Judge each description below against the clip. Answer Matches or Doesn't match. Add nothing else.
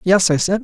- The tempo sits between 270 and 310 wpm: Matches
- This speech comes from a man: Matches